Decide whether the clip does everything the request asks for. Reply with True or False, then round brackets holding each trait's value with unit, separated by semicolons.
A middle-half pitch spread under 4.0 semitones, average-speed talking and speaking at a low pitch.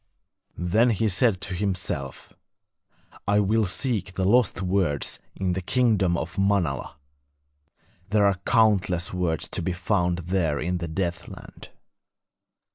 False (2.8 semitones; 125 wpm; 95 Hz)